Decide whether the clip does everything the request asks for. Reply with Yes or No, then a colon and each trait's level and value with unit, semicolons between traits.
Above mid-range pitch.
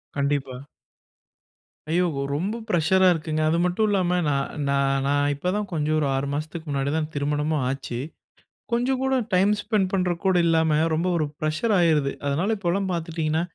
No: medium, 160 Hz